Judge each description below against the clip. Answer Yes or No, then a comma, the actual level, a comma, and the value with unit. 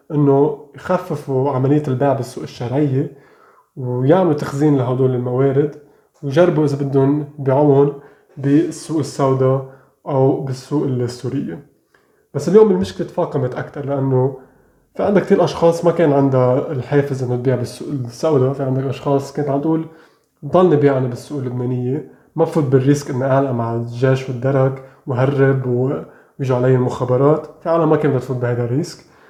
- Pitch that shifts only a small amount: Yes, narrow, 2.2 semitones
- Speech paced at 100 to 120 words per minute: No, fast, 135 wpm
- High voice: No, medium, 140 Hz